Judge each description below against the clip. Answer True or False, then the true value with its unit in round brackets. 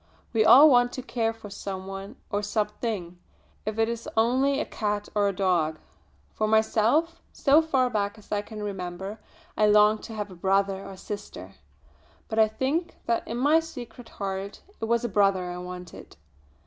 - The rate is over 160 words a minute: True (180 wpm)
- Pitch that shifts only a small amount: False (3.2 semitones)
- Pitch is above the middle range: True (210 Hz)